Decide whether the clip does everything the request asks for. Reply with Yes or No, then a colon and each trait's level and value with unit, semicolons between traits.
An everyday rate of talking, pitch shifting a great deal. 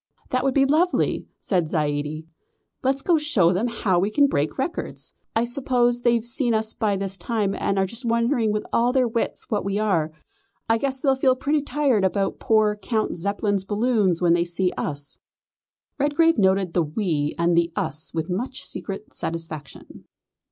Yes: average, 185 wpm; wide, 5.9 semitones